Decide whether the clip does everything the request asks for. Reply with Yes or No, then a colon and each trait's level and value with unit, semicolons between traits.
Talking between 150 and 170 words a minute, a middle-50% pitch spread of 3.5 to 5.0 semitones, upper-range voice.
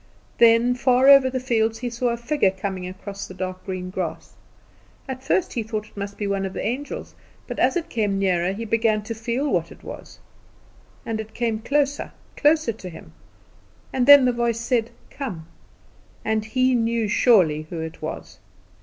No: average, 185 wpm; average, 4.1 semitones; high, 225 Hz